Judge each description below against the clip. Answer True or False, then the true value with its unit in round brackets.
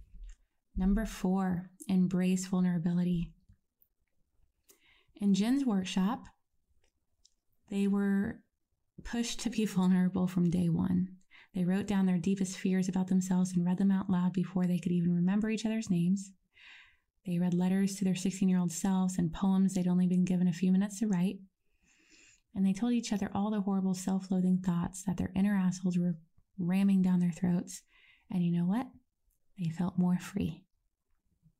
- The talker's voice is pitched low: False (185 Hz)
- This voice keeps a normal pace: True (160 wpm)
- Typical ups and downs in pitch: False (1.6 semitones)